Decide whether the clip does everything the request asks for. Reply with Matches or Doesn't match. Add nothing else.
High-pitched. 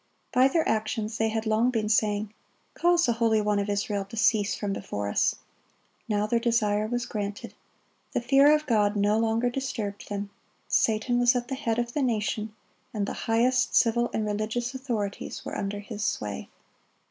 Matches